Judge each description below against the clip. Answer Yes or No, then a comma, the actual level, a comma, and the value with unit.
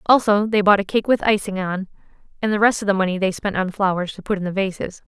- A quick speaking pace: Yes, fast, 270 wpm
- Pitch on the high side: Yes, high, 200 Hz